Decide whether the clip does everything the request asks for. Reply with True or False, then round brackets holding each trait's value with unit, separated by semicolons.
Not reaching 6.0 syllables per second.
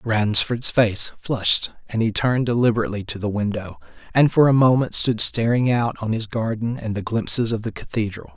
True (5.3 syllables/s)